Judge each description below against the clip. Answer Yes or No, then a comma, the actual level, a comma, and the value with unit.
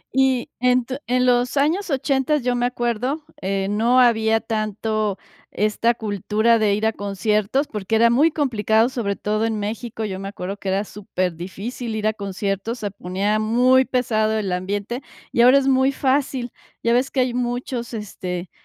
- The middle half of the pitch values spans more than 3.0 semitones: Yes, average, 3.4 semitones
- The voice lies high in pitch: Yes, high, 225 Hz